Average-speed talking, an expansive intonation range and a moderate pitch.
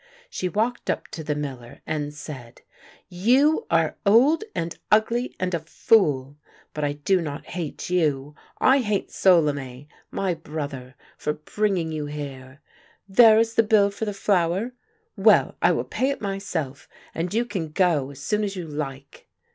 Yes: average, 170 wpm; wide, 6.2 semitones; medium, 170 Hz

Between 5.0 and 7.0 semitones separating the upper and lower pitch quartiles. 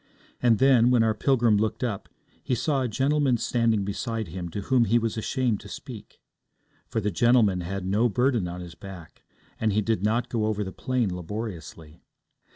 No: average, 3.9 semitones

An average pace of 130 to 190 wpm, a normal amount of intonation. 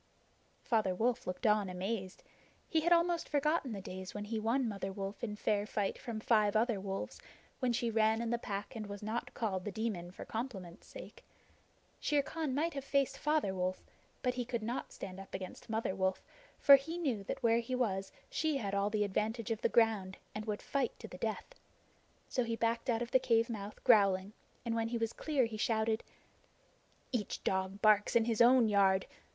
No: average, 200 wpm; average, 3.3 semitones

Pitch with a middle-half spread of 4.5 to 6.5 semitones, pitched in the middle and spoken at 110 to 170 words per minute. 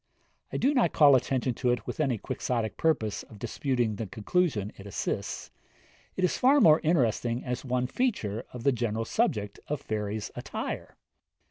No: wide, 5.4 semitones; low, 125 Hz; average, 165 wpm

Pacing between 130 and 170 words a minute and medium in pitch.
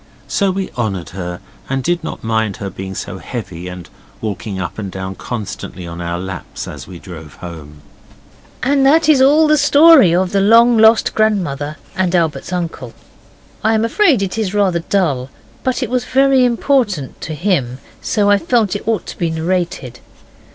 No: average, 180 wpm; medium, 175 Hz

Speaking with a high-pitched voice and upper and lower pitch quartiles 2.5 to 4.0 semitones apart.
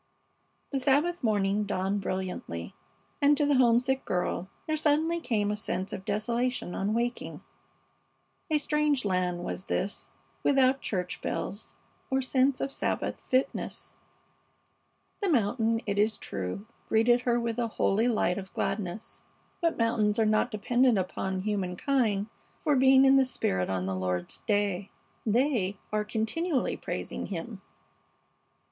No: high, 220 Hz; average, 5.2 semitones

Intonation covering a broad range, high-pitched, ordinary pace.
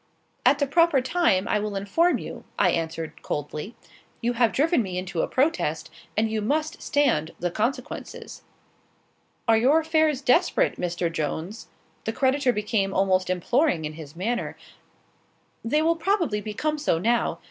Yes: wide, 7.9 semitones; high, 225 Hz; average, 150 wpm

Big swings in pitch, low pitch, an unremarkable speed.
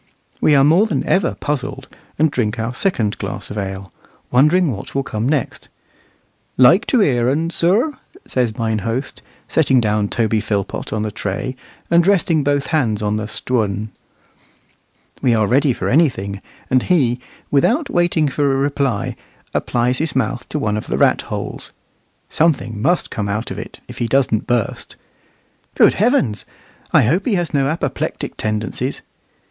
Yes: wide, 6.1 semitones; low, 130 Hz; average, 160 wpm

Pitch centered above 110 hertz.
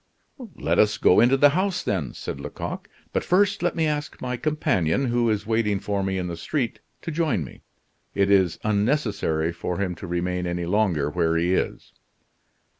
No: low, 100 Hz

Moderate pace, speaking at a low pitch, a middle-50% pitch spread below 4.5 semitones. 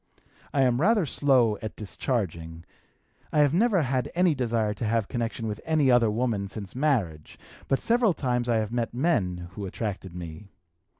No: average, 170 wpm; low, 120 Hz; average, 5.1 semitones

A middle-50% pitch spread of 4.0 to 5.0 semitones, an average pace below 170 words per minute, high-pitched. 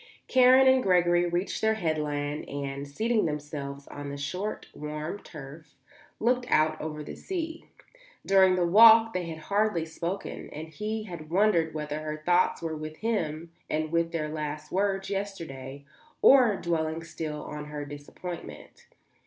No: average, 4.6 semitones; average, 150 wpm; medium, 165 Hz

